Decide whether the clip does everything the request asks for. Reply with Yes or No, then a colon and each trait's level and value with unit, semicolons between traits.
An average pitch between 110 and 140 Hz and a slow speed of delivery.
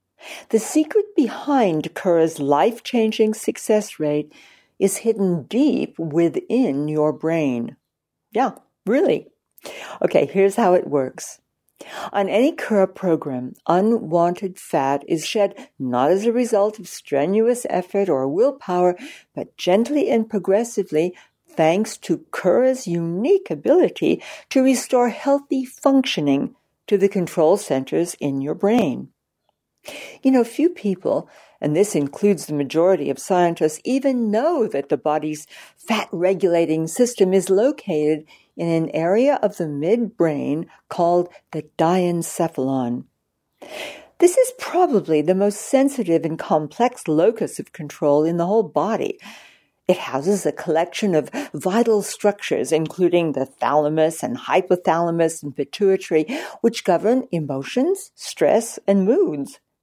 No: medium, 185 Hz; slow, 125 wpm